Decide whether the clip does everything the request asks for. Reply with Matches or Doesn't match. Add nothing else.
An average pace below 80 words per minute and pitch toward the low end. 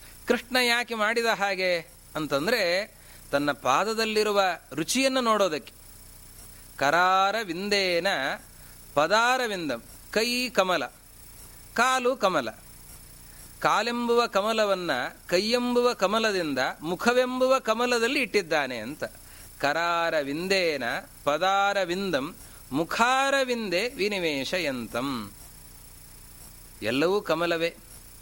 Doesn't match